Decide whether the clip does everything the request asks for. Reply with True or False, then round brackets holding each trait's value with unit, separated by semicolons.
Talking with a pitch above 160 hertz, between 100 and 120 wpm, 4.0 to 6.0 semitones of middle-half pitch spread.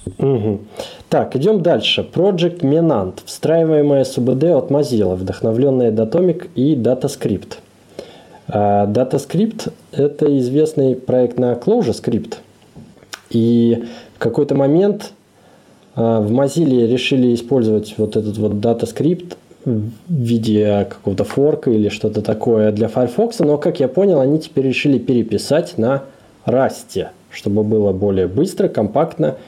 False (125 Hz; 115 wpm; 5.4 semitones)